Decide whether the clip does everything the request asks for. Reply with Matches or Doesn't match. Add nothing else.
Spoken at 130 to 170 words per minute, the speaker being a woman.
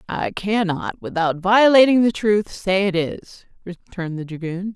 Matches